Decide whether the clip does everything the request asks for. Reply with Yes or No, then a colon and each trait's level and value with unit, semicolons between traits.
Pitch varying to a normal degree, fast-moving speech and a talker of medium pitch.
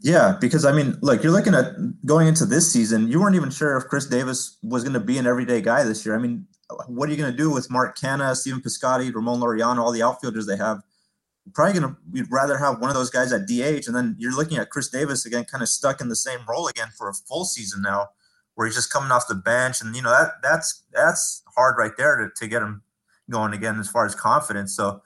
No: average, 4.2 semitones; fast, 255 wpm; low, 130 Hz